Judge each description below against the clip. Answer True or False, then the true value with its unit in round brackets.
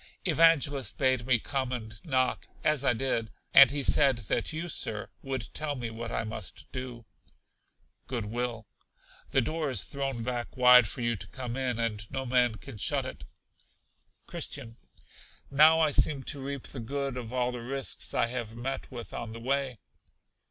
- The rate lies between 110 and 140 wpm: False (175 wpm)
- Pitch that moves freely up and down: False (2.9 semitones)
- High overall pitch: False (125 Hz)